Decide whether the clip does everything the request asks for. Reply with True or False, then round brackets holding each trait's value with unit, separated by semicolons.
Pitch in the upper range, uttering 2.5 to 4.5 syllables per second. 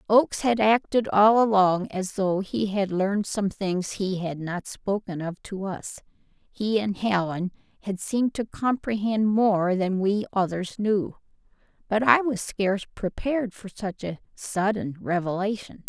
True (200 Hz; 4.2 syllables/s)